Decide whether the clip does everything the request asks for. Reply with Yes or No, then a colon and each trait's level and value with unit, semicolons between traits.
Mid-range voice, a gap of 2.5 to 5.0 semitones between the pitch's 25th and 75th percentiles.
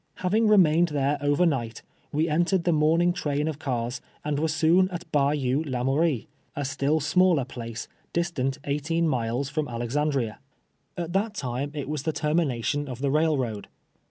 Yes: medium, 150 Hz; average, 3.7 semitones